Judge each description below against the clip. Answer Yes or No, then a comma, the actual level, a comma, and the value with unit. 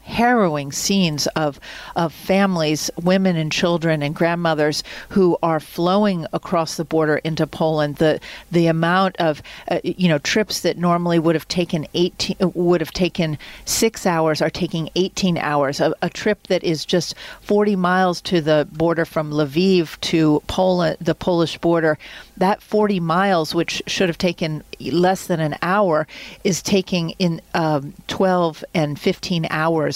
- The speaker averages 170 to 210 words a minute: No, average, 155 wpm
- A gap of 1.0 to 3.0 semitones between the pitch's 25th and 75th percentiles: Yes, average, 2.7 semitones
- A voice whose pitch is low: No, medium, 170 Hz